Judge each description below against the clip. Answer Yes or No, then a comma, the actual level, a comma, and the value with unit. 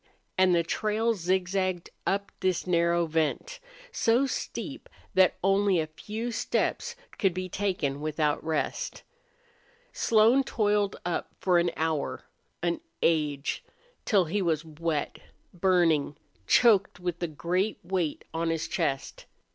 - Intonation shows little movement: No, average, 3.7 semitones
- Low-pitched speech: No, medium, 180 Hz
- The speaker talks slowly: Yes, slow, 125 wpm